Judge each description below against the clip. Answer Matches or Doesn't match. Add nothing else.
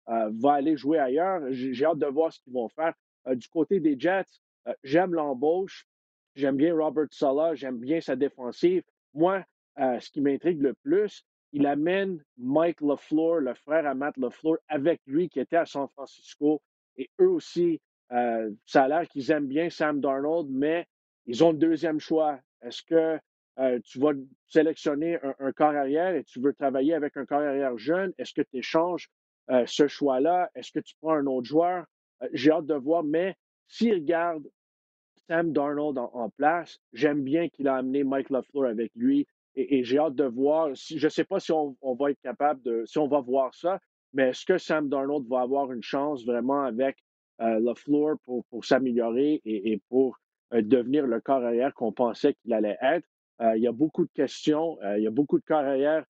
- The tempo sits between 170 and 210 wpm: Matches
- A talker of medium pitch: Matches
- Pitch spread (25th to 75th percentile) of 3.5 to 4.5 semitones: Matches